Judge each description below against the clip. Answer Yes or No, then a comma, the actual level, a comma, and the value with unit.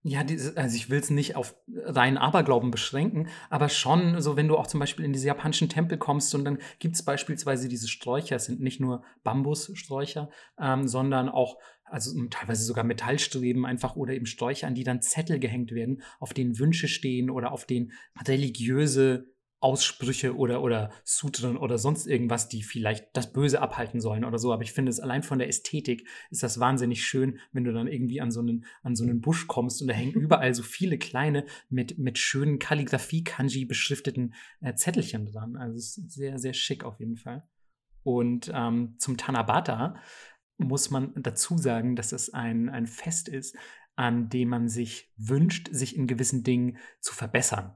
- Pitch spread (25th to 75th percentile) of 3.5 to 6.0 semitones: No, average, 2.9 semitones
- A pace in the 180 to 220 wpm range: Yes, average, 185 wpm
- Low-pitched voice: Yes, low, 130 Hz